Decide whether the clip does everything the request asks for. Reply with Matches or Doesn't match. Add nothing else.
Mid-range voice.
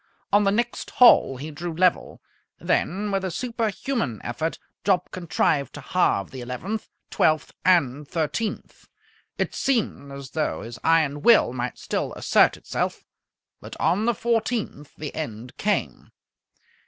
Matches